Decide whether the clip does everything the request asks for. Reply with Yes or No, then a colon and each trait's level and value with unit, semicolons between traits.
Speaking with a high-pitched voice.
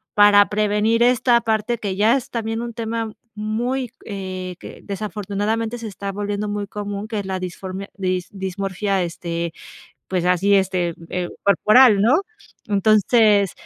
Yes: high, 205 Hz